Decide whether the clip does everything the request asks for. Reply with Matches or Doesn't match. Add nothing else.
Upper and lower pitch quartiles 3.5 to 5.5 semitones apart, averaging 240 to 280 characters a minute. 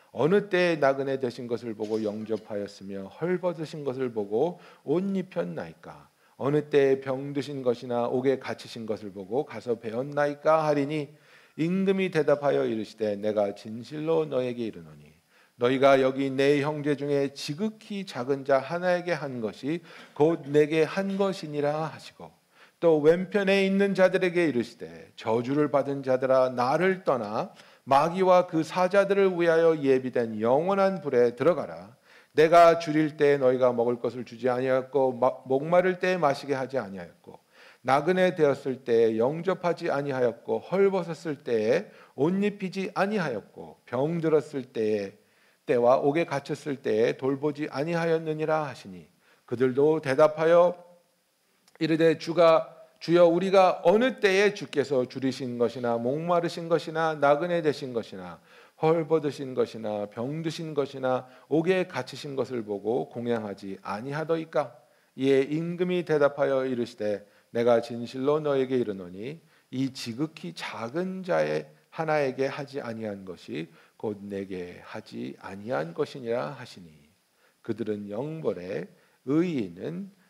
Doesn't match